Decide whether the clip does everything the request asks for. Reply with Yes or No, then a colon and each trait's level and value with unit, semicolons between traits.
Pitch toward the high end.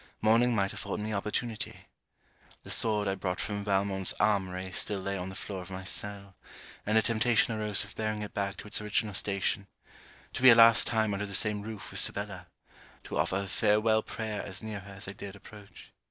No: low, 105 Hz